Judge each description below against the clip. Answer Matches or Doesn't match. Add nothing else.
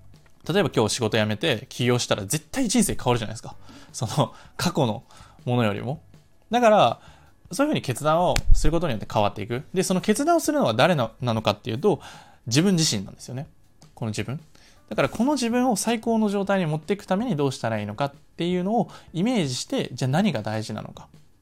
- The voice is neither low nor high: Matches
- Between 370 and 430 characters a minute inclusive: Matches